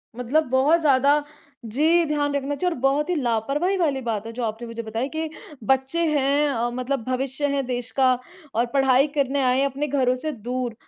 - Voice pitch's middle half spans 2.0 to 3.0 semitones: Yes, average, 2.7 semitones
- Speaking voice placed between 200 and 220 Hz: No, very high, 270 Hz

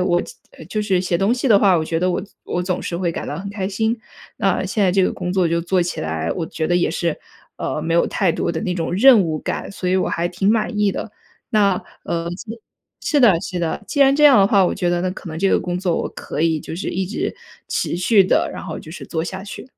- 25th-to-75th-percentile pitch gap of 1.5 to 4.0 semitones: Yes, average, 2.9 semitones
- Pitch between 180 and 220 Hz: Yes, medium, 185 Hz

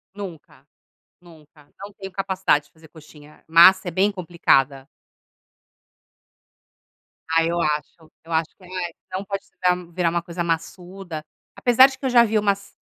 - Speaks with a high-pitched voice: No, medium, 175 Hz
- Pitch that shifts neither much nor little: Yes, average, 3.2 semitones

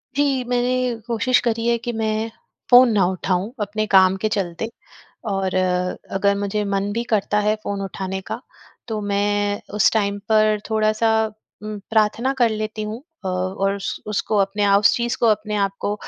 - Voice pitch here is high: Yes, high, 210 Hz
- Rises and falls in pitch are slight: Yes, narrow, 1.9 semitones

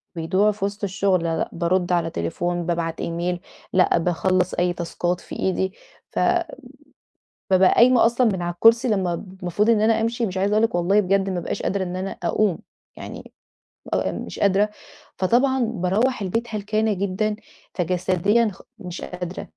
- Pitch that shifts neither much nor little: Yes, average, 3.2 semitones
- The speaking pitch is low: No, high, 190 Hz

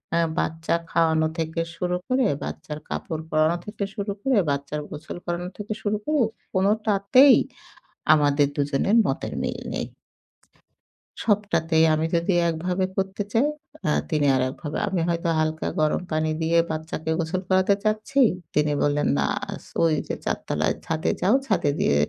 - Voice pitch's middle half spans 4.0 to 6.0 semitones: Yes, average, 4.3 semitones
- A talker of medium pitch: Yes, medium, 165 Hz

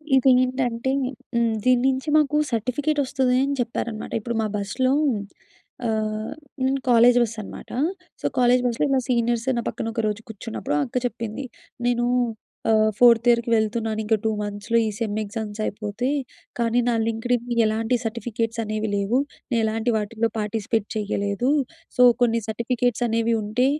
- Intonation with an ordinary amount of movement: No, narrow, 2.2 semitones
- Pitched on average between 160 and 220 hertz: No, high, 230 Hz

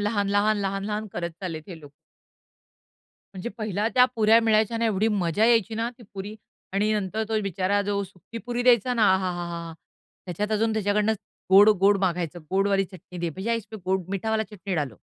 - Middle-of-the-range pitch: No, high, 205 Hz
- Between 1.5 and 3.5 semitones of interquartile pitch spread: Yes, average, 2.7 semitones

